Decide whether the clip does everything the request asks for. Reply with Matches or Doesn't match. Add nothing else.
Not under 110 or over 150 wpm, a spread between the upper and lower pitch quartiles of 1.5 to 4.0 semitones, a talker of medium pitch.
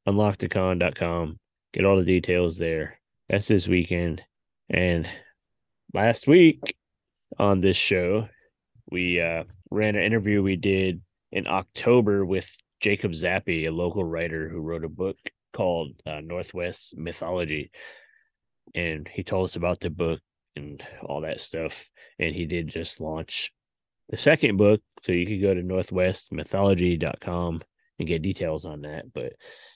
Doesn't match